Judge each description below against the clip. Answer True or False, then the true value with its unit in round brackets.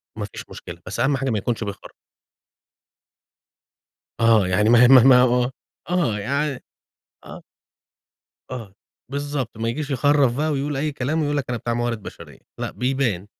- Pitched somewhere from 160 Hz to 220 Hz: False (125 Hz)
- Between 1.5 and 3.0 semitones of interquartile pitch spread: False (3.7 semitones)